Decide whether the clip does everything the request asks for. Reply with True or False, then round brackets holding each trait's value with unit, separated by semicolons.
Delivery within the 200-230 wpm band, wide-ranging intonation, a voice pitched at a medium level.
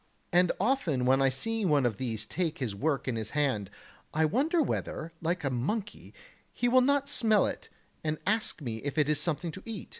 True (205 wpm; 8.4 semitones; 160 Hz)